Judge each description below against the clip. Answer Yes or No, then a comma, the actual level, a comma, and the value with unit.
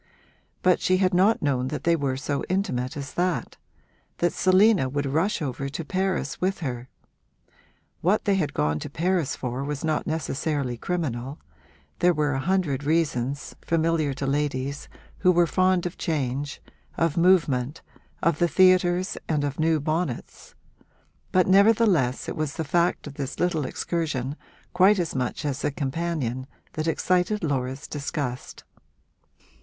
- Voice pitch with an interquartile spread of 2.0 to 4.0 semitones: No, average, 4.5 semitones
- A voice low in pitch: No, medium, 155 Hz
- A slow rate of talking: No, average, 150 wpm